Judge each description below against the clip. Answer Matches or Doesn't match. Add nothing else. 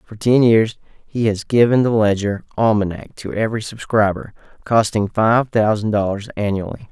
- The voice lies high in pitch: Doesn't match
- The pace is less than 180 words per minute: Matches